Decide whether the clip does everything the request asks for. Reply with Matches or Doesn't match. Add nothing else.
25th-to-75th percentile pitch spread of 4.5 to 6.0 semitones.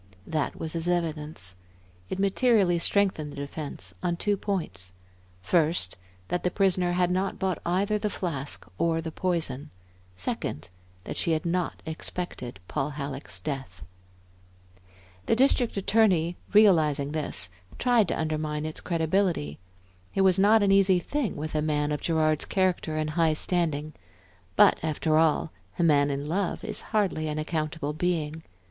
Doesn't match